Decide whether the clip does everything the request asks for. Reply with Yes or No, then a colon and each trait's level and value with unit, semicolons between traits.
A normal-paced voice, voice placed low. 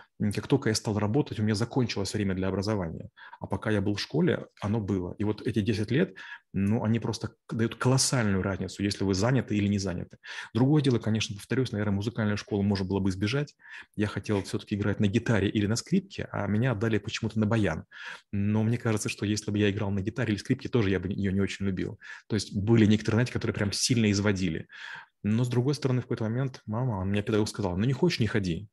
No: fast, 225 wpm; low, 105 Hz